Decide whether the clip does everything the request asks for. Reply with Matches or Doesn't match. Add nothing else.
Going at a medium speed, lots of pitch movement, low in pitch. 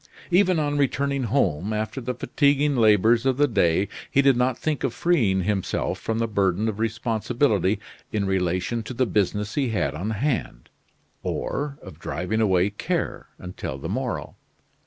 Matches